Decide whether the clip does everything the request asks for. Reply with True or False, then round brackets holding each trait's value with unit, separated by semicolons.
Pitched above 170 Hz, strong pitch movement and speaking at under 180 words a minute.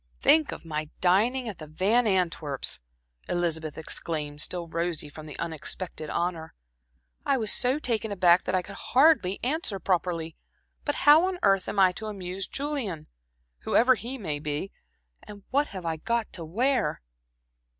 True (185 Hz; 6.4 semitones; 160 wpm)